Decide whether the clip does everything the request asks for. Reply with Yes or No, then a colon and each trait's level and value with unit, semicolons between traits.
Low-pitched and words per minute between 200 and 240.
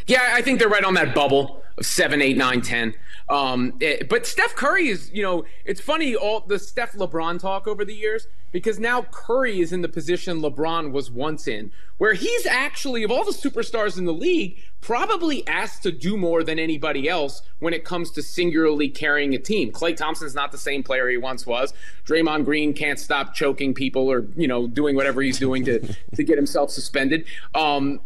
No: medium, 165 Hz; fast, 205 wpm